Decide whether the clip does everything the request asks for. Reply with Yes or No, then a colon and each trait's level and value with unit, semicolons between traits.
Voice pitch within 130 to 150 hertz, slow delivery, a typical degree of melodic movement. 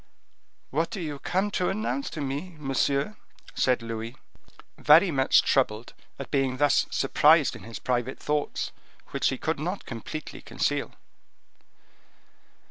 Yes: medium, 140 Hz; slow, 130 wpm; average, 4.4 semitones